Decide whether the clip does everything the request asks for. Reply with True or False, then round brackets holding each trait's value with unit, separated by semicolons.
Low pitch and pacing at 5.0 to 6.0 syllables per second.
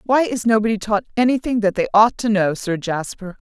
False (215 Hz; 5.5 syllables/s)